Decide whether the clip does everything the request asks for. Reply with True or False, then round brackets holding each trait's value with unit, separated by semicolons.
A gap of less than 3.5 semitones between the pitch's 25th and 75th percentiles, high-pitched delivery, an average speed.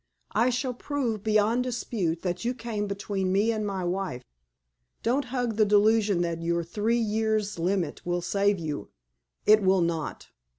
False (4.2 semitones; 205 Hz; 160 wpm)